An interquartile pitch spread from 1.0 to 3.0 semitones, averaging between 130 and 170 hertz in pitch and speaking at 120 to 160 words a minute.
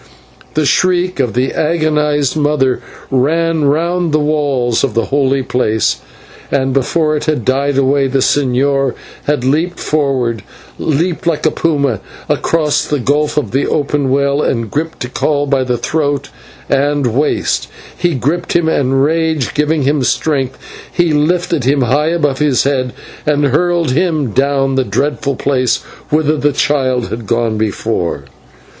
Yes: average, 2.7 semitones; medium, 140 Hz; average, 150 wpm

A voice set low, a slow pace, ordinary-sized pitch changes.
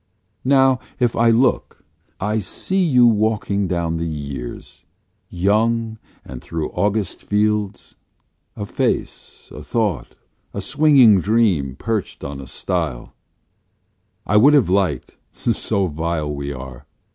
No: low, 100 Hz; slow, 120 wpm; wide, 6.3 semitones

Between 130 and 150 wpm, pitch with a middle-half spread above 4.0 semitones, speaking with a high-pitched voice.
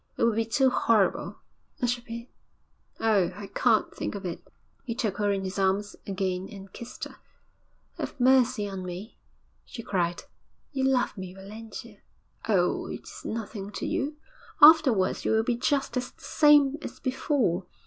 No: average, 165 wpm; average, 4.6 semitones; high, 220 Hz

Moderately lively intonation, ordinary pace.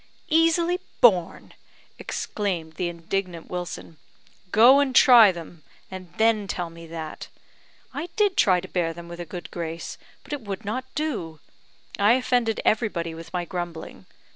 No: wide, 5.9 semitones; average, 150 wpm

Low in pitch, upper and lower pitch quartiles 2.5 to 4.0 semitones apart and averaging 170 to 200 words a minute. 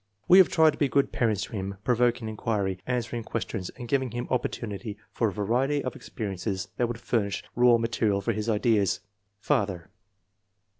Yes: low, 115 Hz; average, 3.3 semitones; average, 180 wpm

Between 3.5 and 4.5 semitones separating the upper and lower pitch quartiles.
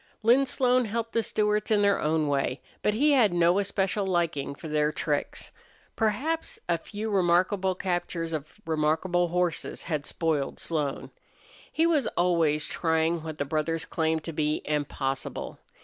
No: average, 5.1 semitones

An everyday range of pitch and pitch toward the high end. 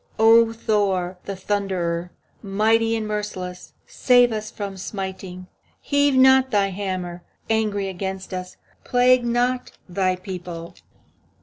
Yes: average, 3.5 semitones; high, 200 Hz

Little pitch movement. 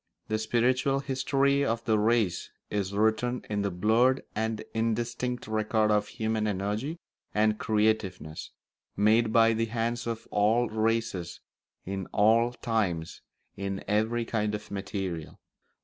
Yes: narrow, 2.2 semitones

